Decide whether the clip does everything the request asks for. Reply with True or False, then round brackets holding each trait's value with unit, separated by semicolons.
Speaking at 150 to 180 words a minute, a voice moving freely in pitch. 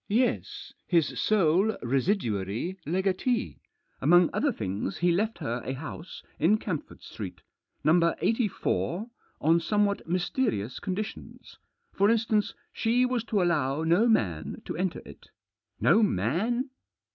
False (135 wpm; 6.1 semitones)